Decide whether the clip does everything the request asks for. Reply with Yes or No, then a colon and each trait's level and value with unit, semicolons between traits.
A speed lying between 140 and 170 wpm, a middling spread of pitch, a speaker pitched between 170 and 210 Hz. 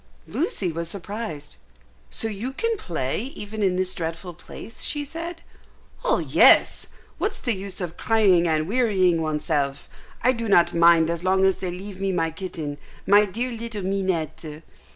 Yes: average, 160 wpm; average, 4.7 semitones; medium, 185 Hz